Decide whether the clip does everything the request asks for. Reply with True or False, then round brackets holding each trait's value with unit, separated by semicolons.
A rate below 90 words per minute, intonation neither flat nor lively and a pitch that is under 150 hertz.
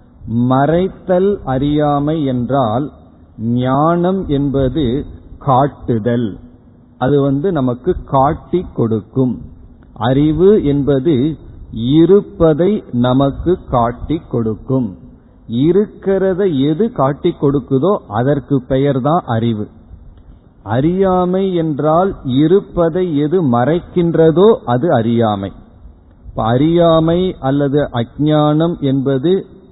False (75 wpm; 5.7 semitones; 140 Hz)